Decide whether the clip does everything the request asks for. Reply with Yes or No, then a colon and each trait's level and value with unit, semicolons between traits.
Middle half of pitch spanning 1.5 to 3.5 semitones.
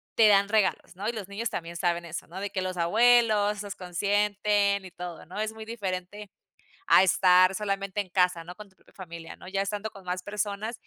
Yes: narrow, 2.4 semitones